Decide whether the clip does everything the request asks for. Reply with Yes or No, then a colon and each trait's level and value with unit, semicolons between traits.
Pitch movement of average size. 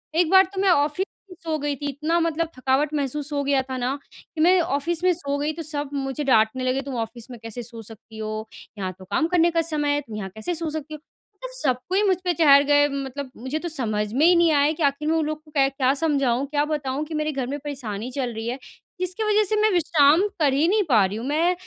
Yes: average, 4.0 semitones